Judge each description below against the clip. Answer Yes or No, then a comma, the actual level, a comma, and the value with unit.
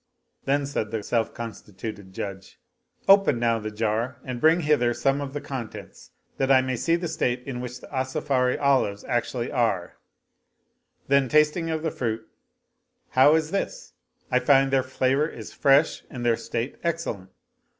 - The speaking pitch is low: Yes, low, 130 Hz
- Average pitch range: Yes, average, 3.7 semitones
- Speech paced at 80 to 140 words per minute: No, average, 165 wpm